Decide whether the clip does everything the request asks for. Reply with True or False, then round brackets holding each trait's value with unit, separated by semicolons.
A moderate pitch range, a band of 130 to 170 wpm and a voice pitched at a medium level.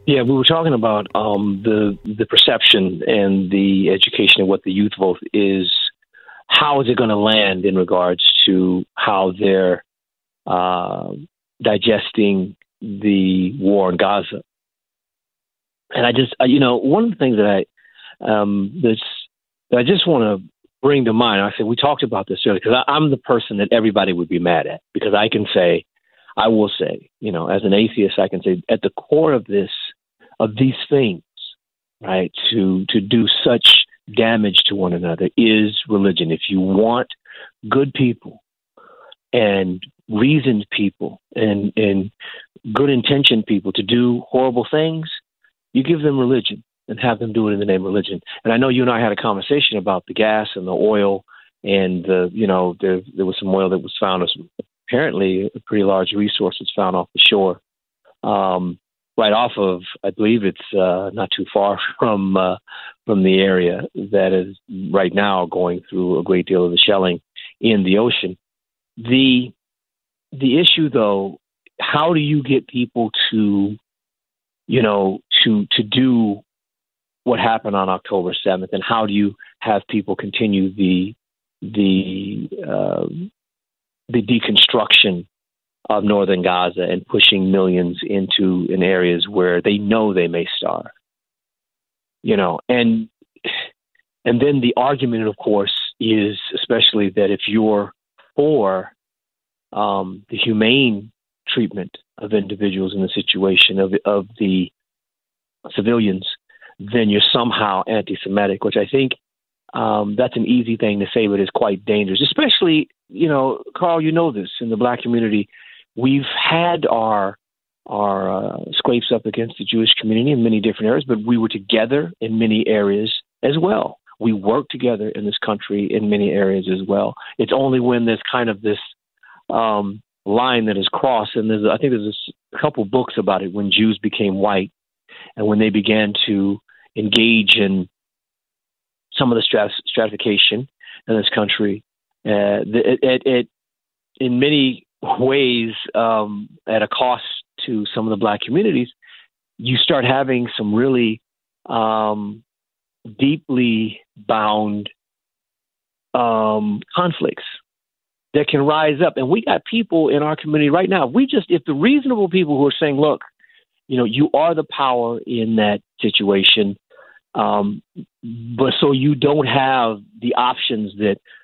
False (4.0 semitones; 160 wpm; 105 Hz)